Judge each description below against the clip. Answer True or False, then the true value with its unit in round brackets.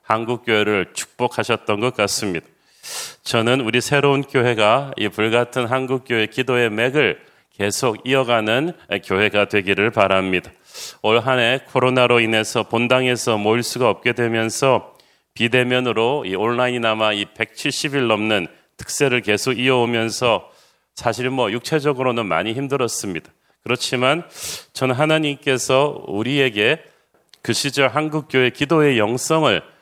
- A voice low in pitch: True (120 Hz)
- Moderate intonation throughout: True (3.1 semitones)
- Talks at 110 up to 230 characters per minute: False (300 characters per minute)